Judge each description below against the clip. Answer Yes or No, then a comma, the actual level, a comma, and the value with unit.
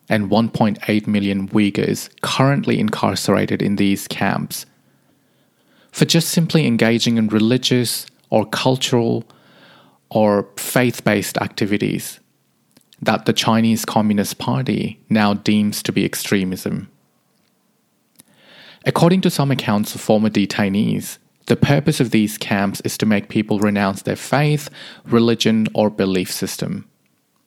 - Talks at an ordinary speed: No, slow, 120 wpm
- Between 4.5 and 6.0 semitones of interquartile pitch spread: No, average, 3.5 semitones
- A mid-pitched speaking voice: No, low, 110 Hz